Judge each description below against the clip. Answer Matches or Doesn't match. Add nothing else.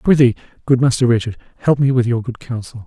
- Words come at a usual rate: Doesn't match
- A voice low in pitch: Matches